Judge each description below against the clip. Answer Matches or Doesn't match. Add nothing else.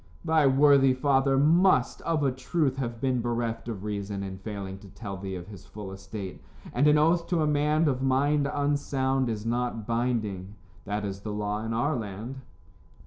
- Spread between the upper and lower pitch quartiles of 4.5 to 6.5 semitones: Matches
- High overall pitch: Doesn't match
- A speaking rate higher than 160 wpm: Matches